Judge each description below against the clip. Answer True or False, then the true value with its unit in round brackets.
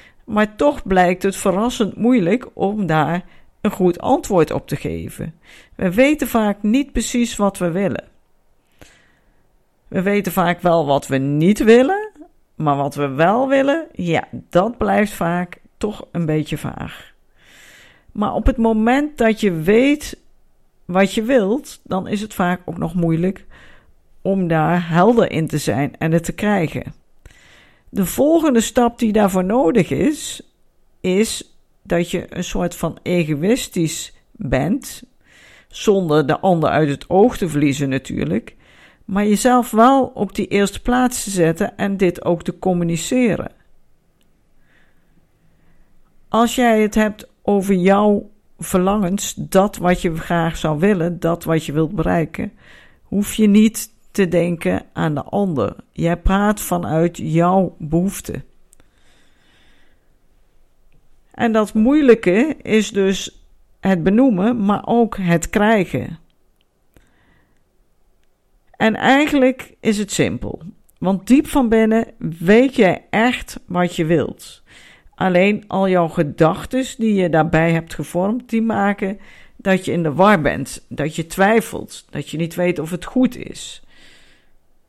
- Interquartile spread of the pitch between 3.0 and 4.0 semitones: False (4.7 semitones)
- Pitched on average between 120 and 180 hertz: False (195 Hz)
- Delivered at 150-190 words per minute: False (135 wpm)